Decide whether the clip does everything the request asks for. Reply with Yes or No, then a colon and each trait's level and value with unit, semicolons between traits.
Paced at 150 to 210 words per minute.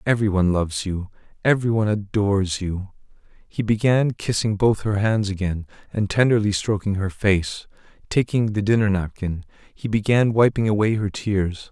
Yes: average, 155 wpm